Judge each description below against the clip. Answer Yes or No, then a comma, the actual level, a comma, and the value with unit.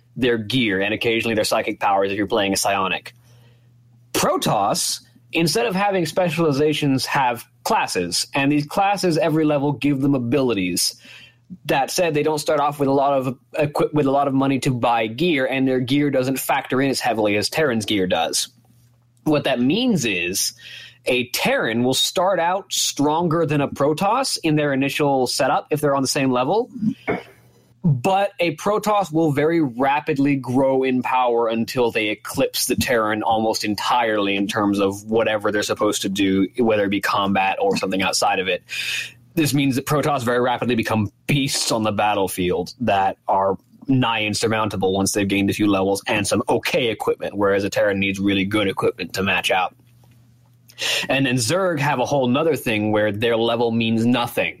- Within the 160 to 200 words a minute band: Yes, average, 175 wpm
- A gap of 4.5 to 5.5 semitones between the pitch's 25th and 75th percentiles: Yes, average, 5.0 semitones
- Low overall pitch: Yes, low, 125 Hz